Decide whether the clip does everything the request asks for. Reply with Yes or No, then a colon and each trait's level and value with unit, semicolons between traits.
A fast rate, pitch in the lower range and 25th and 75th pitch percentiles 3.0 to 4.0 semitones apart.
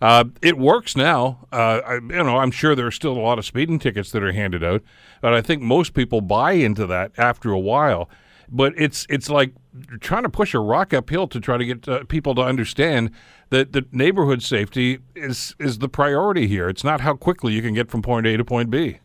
Yes: fast, 235 wpm; low, 125 Hz; average, 3.6 semitones